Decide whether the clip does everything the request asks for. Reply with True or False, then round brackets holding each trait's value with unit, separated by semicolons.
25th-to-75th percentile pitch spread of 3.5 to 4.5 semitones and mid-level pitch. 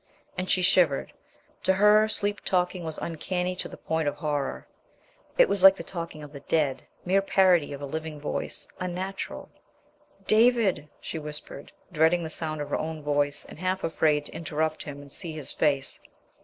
True (3.8 semitones; 160 Hz)